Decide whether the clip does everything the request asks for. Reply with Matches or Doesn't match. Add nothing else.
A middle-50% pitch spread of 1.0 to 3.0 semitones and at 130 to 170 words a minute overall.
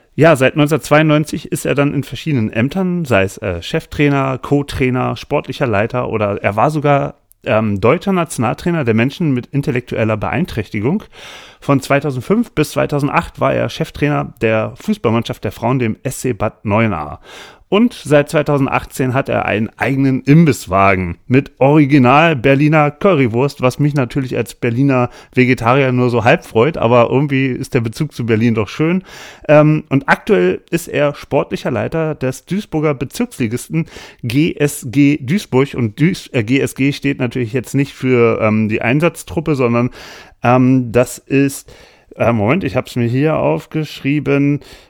Doesn't match